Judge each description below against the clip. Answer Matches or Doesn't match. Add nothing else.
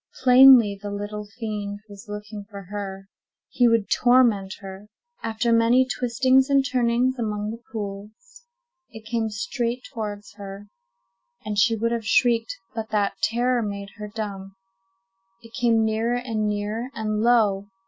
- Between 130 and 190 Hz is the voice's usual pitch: Doesn't match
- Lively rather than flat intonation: Doesn't match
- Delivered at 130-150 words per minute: Matches